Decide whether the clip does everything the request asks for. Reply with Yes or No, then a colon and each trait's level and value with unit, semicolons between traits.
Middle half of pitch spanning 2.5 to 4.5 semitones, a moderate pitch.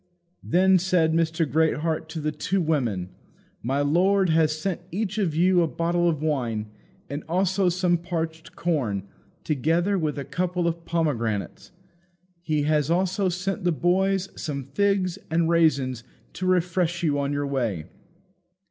Yes: average, 3.4 semitones; medium, 165 Hz